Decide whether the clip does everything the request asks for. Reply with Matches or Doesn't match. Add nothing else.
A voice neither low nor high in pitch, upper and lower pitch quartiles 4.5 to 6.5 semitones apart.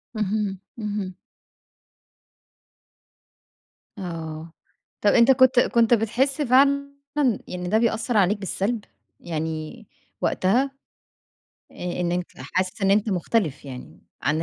Doesn't match